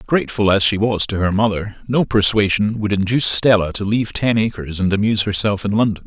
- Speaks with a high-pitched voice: No, low, 105 Hz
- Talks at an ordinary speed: No, fast, 210 wpm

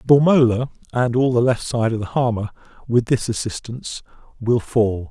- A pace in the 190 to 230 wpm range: No, average, 175 wpm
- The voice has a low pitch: Yes, low, 120 Hz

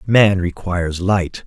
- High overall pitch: No, very low, 95 Hz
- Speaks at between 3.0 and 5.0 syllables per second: Yes, 3.7 syllables/s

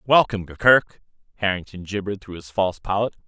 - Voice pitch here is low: Yes, low, 100 Hz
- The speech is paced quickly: No, average, 145 wpm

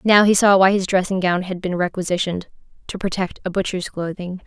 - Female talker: Yes, female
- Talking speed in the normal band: Yes, average, 190 wpm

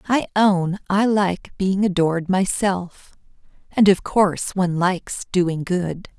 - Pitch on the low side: No, medium, 185 Hz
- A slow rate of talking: Yes, slow, 125 wpm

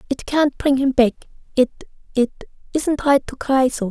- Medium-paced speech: Yes, average, 155 wpm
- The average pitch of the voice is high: Yes, very high, 265 Hz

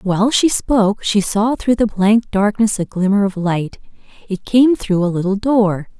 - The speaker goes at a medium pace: Yes, average, 190 wpm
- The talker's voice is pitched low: No, high, 205 Hz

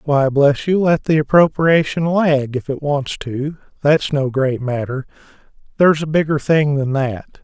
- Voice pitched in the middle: Yes, medium, 145 Hz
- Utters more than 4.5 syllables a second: No, 4.4 syllables/s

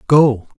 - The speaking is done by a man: Yes, male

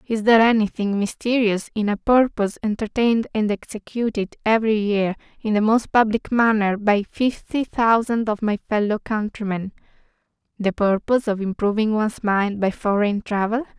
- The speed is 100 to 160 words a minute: Yes, average, 140 wpm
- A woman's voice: Yes, female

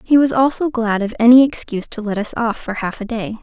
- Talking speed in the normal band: No, fast, 265 wpm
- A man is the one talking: No, female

